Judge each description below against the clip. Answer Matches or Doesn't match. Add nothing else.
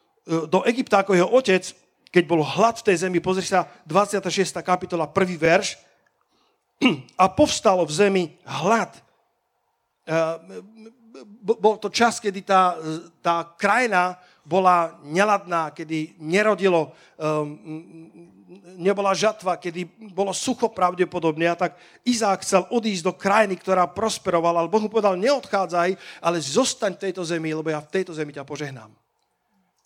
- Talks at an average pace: Matches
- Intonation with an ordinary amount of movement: Matches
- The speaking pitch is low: Doesn't match